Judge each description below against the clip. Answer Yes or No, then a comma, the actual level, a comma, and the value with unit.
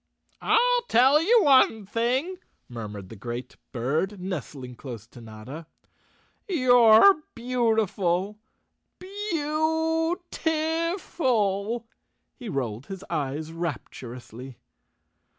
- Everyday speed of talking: No, slow, 90 wpm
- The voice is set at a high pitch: Yes, high, 210 Hz